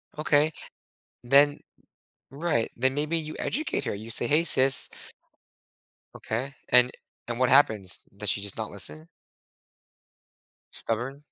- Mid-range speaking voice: No, low, 130 Hz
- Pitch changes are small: No, average, 4.4 semitones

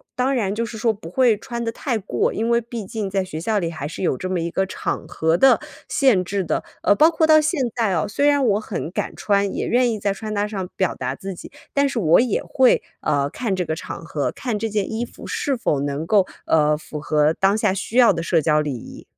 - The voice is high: Yes, high, 200 Hz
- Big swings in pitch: Yes, wide, 5.9 semitones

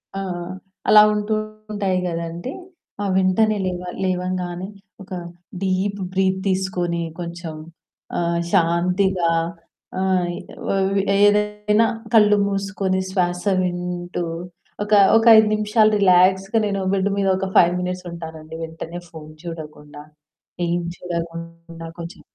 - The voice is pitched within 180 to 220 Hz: Yes, medium, 185 Hz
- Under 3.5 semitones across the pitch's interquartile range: Yes, narrow, 2.5 semitones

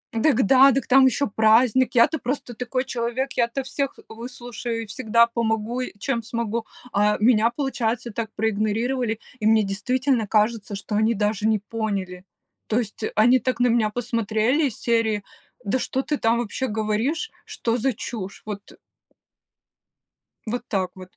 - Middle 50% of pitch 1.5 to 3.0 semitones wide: Yes, average, 2.7 semitones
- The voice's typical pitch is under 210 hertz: No, high, 230 Hz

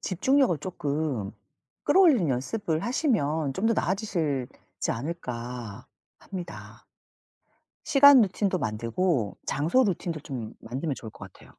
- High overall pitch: No, medium, 160 Hz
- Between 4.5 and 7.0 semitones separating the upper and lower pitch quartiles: No, wide, 8.3 semitones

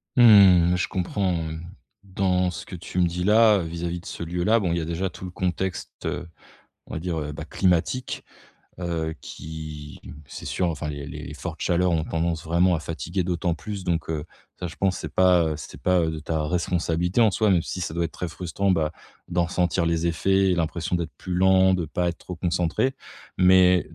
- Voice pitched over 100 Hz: No, very low, 90 Hz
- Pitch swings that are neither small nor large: No, narrow, 2.1 semitones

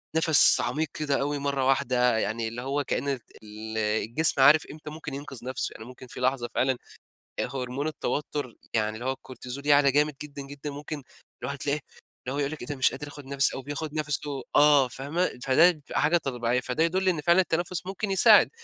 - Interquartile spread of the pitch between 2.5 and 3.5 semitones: Yes, average, 2.9 semitones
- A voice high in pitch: No, medium, 140 Hz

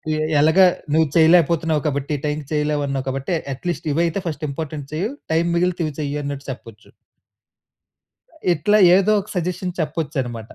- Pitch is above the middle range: No, medium, 155 Hz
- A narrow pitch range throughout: No, average, 3.2 semitones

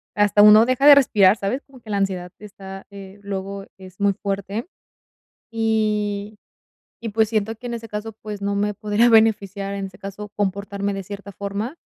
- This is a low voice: No, high, 205 Hz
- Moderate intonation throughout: No, narrow, 1.8 semitones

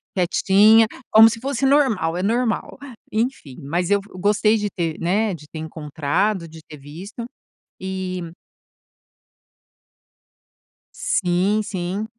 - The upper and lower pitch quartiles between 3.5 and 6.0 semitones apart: Yes, average, 4.4 semitones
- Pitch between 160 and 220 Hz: Yes, high, 190 Hz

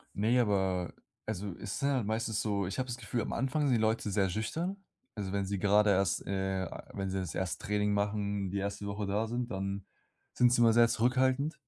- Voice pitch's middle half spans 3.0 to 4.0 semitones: Yes, average, 3.3 semitones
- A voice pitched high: No, low, 105 Hz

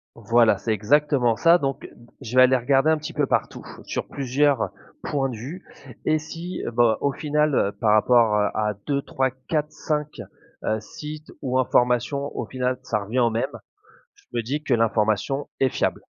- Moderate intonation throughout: Yes, average, 4.2 semitones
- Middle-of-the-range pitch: No, low, 130 Hz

